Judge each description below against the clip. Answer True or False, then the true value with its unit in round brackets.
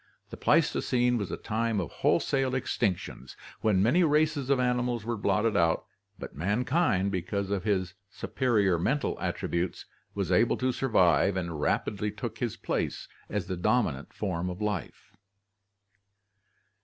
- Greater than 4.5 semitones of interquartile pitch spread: True (5.0 semitones)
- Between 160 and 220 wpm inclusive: False (145 wpm)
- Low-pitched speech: True (105 Hz)